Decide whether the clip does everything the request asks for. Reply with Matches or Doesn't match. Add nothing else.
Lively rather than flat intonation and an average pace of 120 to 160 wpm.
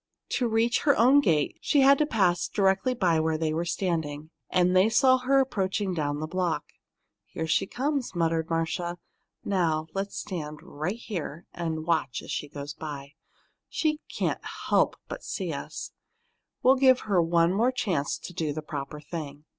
Doesn't match